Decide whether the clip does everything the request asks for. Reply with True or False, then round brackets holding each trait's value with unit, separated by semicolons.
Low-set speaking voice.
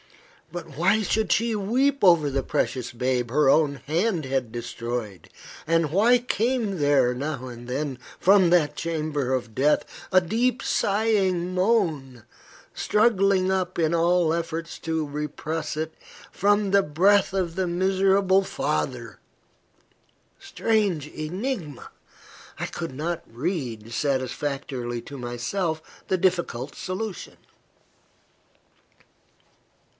False (165 Hz)